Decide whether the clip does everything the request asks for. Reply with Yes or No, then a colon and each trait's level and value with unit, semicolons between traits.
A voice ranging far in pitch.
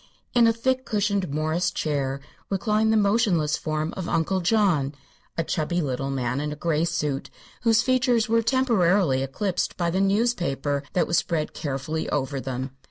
Yes: wide, 6.6 semitones